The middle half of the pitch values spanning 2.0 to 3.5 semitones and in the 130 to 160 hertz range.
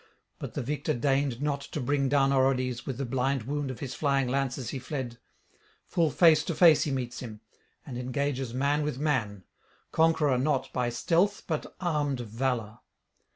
Yes: average, 2.8 semitones; low, 135 Hz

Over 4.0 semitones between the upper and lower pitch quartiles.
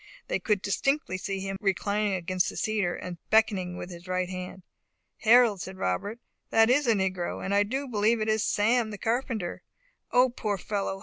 No: average, 3.1 semitones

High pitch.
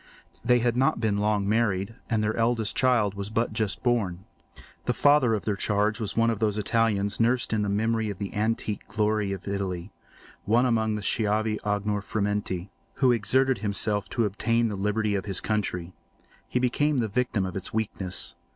No: low, 105 Hz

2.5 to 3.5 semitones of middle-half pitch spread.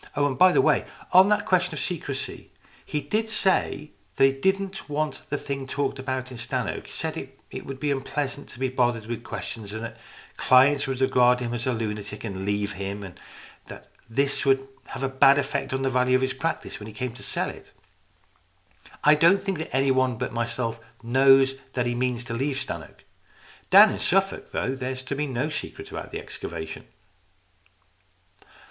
Yes: average, 3.2 semitones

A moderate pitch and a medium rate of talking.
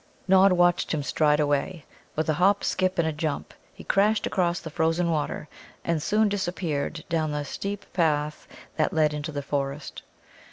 Yes: medium, 160 Hz; average, 170 wpm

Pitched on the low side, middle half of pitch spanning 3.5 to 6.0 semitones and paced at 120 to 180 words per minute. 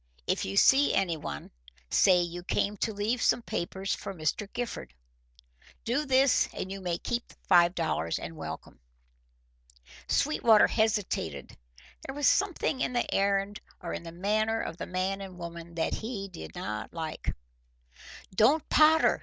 No: high, 195 Hz; average, 5.1 semitones; average, 155 wpm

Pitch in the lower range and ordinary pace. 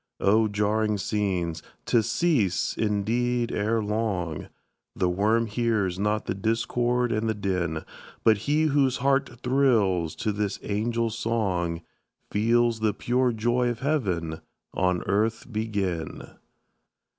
No: low, 110 Hz; slow, 120 wpm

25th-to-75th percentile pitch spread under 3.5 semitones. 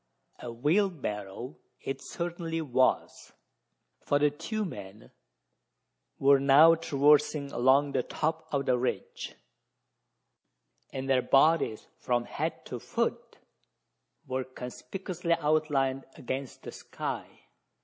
No: average, 3.8 semitones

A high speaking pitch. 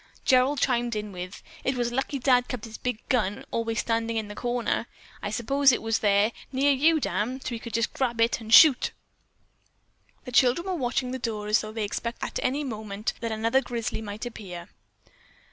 Yes: high, 235 Hz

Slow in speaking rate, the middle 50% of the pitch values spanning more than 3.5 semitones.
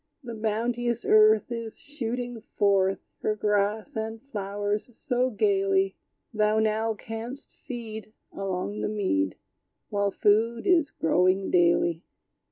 No: slow, 115 wpm; narrow, 2.5 semitones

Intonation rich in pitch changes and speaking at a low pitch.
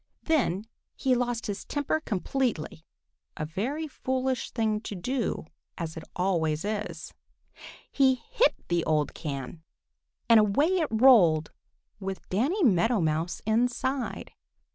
No: wide, 7.3 semitones; high, 220 Hz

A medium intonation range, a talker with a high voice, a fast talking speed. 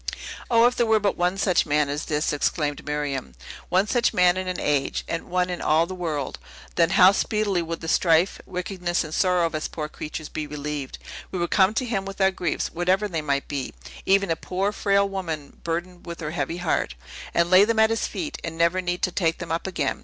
No: average, 3.7 semitones; medium, 175 Hz; fast, 225 wpm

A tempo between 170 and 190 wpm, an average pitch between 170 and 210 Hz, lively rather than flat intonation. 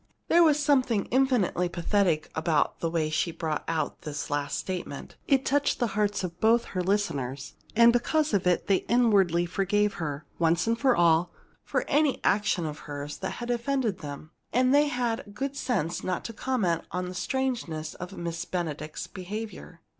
Yes: average, 175 wpm; high, 190 Hz; wide, 6.4 semitones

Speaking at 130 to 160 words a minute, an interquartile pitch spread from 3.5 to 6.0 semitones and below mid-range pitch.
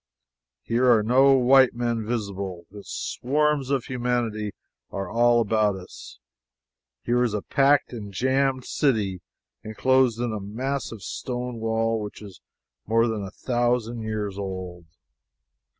No: slow, 135 wpm; average, 3.1 semitones; low, 115 Hz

